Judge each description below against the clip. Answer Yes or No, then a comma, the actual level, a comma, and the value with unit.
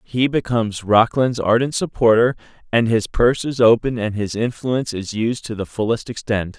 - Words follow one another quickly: No, average, 175 wpm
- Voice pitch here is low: Yes, low, 115 Hz